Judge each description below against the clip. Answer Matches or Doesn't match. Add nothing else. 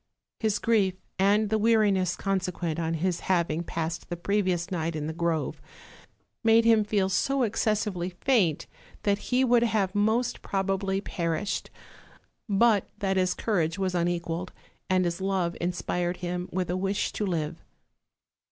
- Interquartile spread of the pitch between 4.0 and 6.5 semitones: Doesn't match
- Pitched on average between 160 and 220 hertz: Matches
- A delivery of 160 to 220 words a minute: Doesn't match